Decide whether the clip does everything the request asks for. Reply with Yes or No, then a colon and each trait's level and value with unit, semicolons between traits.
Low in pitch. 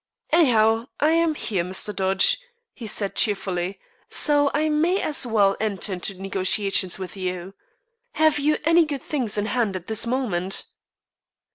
No: high, 215 Hz